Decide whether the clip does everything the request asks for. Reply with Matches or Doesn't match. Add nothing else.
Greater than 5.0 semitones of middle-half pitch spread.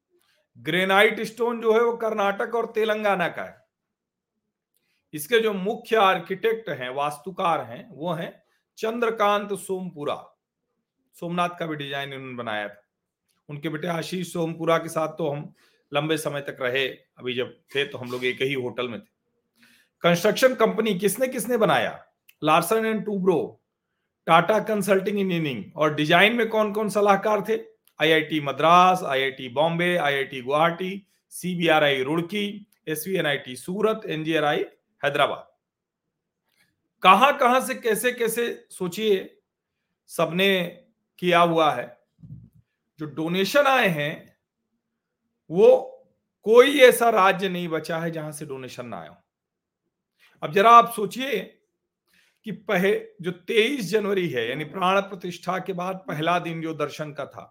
Matches